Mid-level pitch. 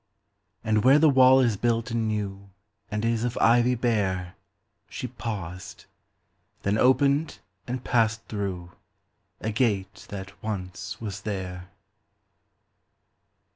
No: low, 110 Hz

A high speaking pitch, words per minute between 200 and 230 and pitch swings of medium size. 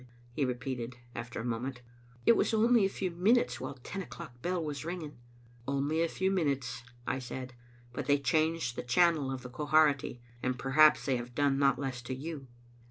No: medium, 140 Hz; fast, 205 wpm; average, 4.4 semitones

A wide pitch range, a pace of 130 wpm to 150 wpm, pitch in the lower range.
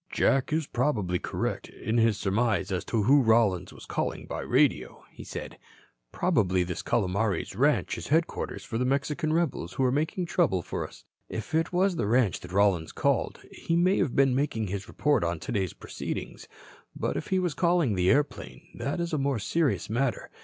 No: wide, 7.4 semitones; average, 190 wpm; low, 120 Hz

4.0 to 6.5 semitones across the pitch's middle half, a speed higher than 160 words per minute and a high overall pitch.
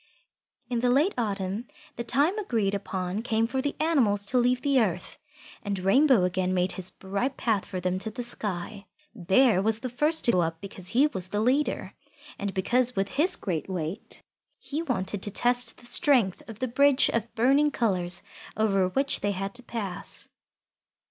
Yes: average, 5.0 semitones; average, 180 wpm; high, 220 Hz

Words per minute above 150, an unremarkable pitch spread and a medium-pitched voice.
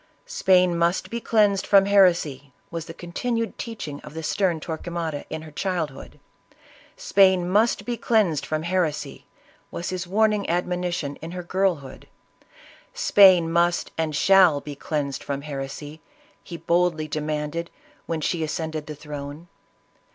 No: average, 145 wpm; average, 3.6 semitones; medium, 170 Hz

